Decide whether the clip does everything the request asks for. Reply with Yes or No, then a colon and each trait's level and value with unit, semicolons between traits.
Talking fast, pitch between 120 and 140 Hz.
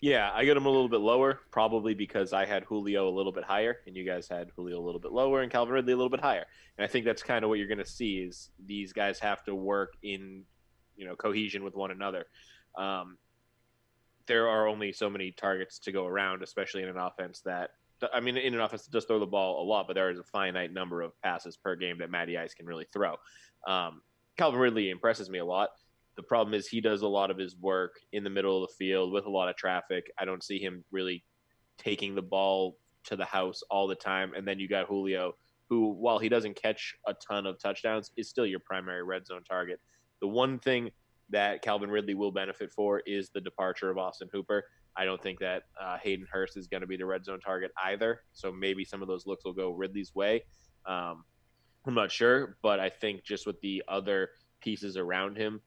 No: fast, 235 wpm; very low, 95 Hz